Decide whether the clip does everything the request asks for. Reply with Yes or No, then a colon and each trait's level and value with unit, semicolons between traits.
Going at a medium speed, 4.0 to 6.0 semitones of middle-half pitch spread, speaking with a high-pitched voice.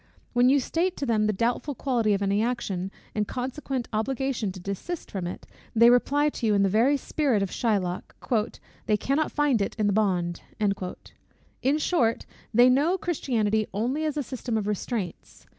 Yes: average, 180 wpm; average, 4.8 semitones; high, 235 Hz